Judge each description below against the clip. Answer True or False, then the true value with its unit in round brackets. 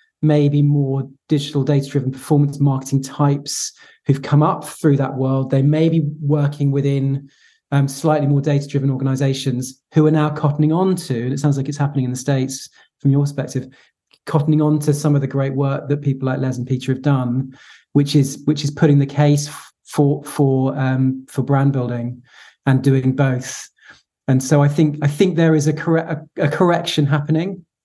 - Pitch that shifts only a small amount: True (1.9 semitones)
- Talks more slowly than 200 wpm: True (185 wpm)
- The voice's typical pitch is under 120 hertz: False (140 Hz)